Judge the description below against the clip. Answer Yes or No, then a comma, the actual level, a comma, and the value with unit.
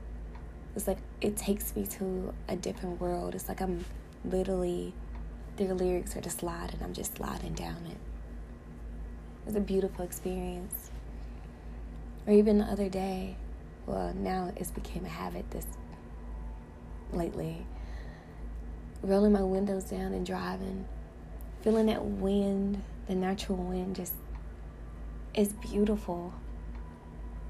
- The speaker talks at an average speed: No, slow, 120 wpm